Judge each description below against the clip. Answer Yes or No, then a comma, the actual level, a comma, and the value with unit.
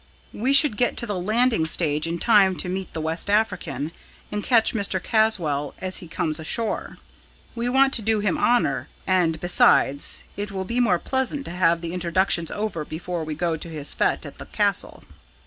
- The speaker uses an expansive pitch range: No, average, 5.0 semitones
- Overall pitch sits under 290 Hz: Yes, medium, 185 Hz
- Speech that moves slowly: No, average, 190 wpm